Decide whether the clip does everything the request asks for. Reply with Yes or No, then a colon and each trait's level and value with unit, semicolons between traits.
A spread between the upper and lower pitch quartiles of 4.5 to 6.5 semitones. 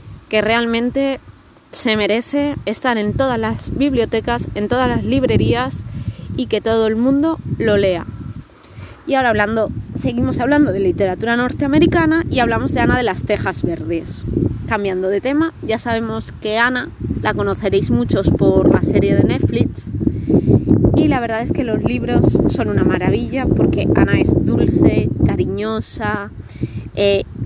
Yes: average, 5.3 semitones